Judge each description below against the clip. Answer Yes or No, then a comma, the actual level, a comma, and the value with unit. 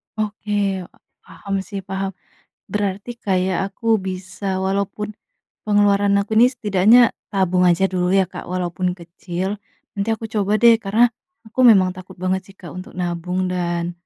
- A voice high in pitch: Yes, high, 195 Hz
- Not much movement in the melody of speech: Yes, narrow, 2.3 semitones